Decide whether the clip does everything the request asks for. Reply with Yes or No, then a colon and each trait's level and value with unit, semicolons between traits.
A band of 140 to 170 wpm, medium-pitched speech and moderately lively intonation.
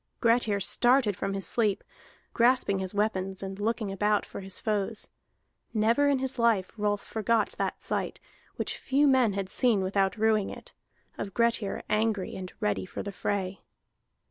No: average, 160 wpm; high, 210 Hz; average, 3.1 semitones